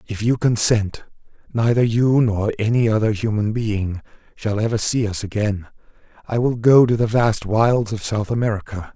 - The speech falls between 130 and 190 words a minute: Yes, average, 165 wpm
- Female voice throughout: No, male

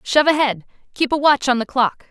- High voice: Yes, very high, 265 Hz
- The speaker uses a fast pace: Yes, fast, 230 wpm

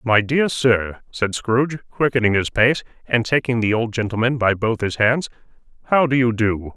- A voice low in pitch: Yes, low, 120 Hz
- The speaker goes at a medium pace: Yes, average, 185 wpm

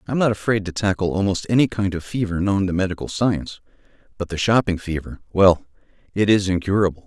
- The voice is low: Yes, very low, 95 Hz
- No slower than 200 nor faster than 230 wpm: No, average, 180 wpm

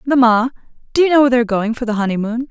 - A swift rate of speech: Yes, fast, 240 wpm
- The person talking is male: No, female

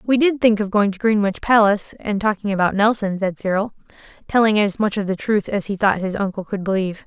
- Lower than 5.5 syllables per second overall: No, 5.9 syllables/s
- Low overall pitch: No, high, 205 Hz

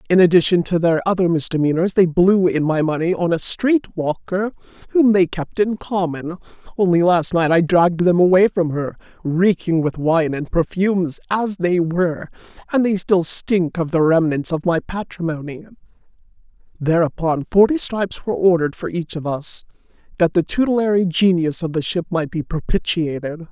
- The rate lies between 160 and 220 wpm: Yes, average, 170 wpm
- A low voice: No, medium, 175 Hz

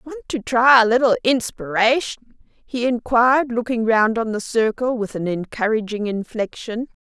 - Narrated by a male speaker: No, female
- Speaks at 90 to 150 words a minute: Yes, average, 145 wpm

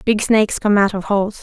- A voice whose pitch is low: No, high, 205 Hz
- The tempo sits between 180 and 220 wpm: No, fast, 255 wpm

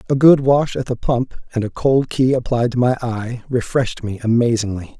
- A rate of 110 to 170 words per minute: No, fast, 205 wpm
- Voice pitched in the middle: No, low, 120 Hz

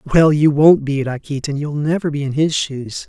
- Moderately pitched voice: Yes, medium, 145 Hz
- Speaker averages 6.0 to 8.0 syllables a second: No, 4.7 syllables/s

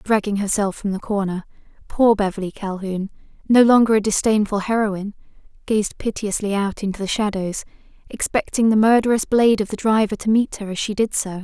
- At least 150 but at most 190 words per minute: Yes, average, 175 wpm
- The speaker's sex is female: Yes, female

